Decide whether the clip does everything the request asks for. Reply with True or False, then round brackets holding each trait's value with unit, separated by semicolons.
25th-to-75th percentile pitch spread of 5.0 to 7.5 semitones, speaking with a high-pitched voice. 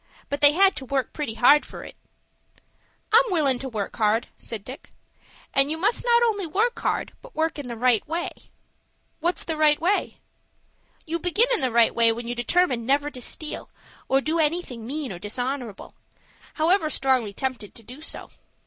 True (5.6 semitones; 285 Hz)